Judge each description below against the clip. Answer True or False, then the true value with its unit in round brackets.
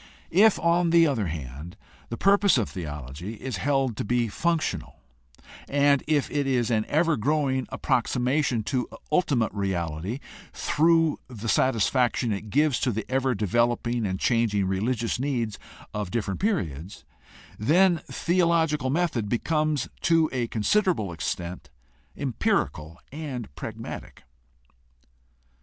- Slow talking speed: True (125 wpm)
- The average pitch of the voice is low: True (125 Hz)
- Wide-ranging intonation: True (6.5 semitones)